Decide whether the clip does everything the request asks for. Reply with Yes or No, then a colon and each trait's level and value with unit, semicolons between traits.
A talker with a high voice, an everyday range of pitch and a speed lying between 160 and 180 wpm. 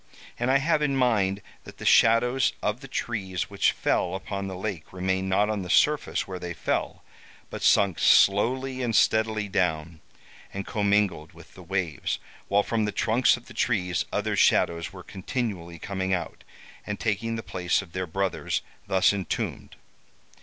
No: low, 100 Hz; average, 3.6 semitones; average, 165 wpm